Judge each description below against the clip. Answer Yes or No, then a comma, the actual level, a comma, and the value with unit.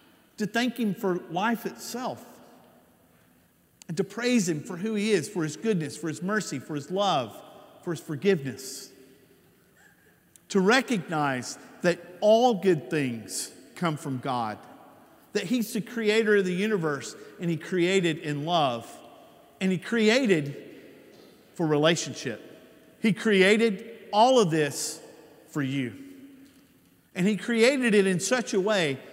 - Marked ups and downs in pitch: Yes, wide, 6.2 semitones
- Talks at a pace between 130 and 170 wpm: Yes, average, 140 wpm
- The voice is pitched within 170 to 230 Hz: Yes, medium, 185 Hz